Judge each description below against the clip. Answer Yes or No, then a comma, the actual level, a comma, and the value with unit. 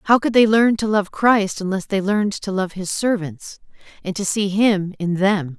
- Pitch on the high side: Yes, high, 200 Hz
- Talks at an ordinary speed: No, fast, 215 wpm